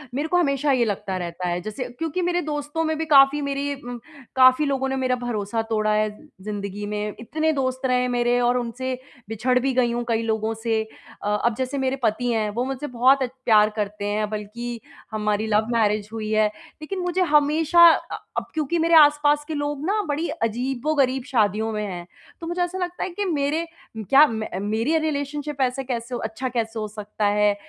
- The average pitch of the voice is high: Yes, very high, 250 Hz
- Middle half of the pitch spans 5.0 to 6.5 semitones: Yes, average, 5.3 semitones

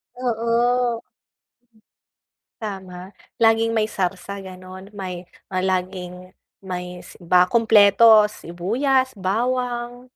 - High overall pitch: Yes, high, 200 Hz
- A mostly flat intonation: No, average, 4.2 semitones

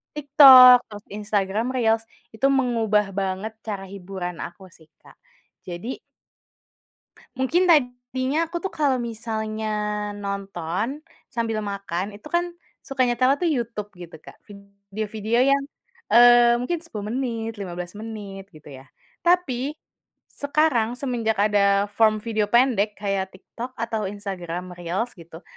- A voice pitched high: Yes, high, 220 Hz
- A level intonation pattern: No, average, 4.2 semitones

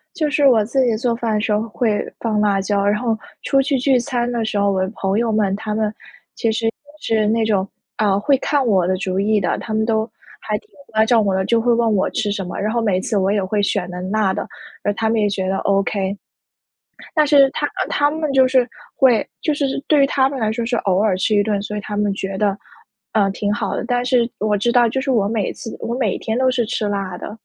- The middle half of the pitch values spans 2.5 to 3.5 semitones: Yes, average, 3.2 semitones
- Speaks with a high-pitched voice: Yes, high, 220 Hz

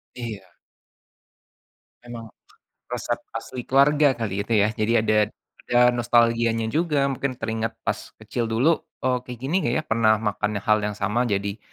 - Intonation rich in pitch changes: No, narrow, 2.5 semitones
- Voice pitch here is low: Yes, low, 115 Hz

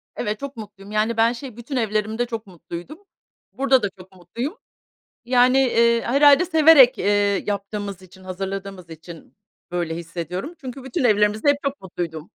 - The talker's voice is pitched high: Yes, high, 215 Hz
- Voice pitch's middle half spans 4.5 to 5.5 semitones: Yes, average, 5.1 semitones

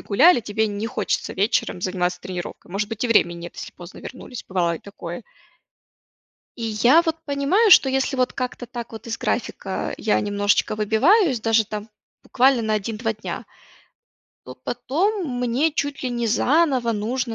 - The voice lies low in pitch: No, high, 230 Hz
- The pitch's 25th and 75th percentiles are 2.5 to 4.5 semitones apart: Yes, average, 4.2 semitones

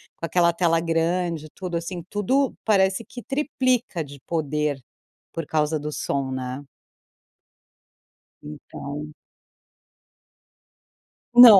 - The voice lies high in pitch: No, medium, 165 Hz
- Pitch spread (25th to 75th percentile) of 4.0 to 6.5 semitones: Yes, average, 4.3 semitones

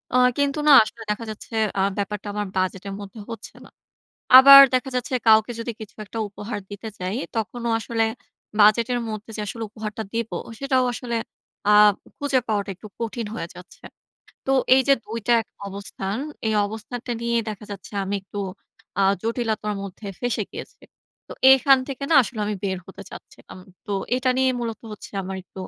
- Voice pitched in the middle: No, high, 220 Hz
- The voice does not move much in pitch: No, average, 3.1 semitones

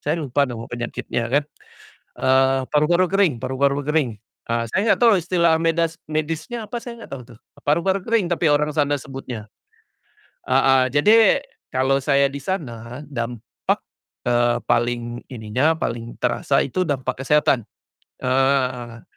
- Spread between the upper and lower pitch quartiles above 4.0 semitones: Yes, average, 4.7 semitones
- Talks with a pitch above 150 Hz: No, low, 135 Hz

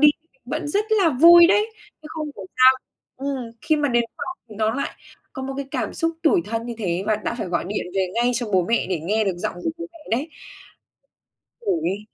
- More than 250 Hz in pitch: Yes, very high, 260 Hz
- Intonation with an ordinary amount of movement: No, wide, 7.0 semitones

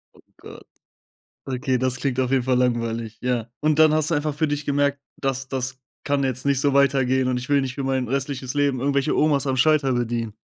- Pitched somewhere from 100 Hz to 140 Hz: Yes, low, 135 Hz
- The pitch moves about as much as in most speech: No, narrow, 2.1 semitones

